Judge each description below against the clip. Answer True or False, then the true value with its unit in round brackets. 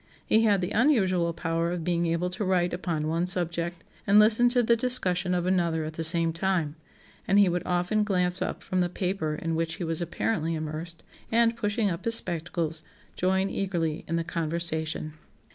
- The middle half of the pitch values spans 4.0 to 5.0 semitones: False (2.8 semitones)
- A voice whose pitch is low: False (175 Hz)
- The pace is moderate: True (190 wpm)